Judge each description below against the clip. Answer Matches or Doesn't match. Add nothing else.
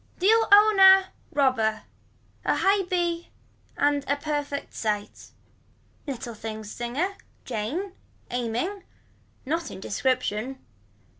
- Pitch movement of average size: Doesn't match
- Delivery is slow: Matches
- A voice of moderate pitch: Doesn't match